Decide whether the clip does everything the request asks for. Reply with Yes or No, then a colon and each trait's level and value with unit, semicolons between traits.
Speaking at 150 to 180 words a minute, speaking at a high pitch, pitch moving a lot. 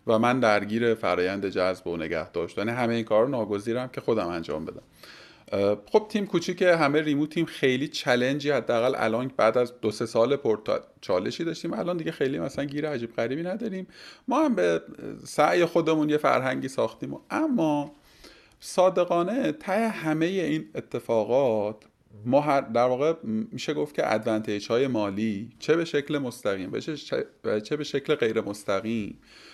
No: fast, 155 wpm; medium, 140 Hz; wide, 6.8 semitones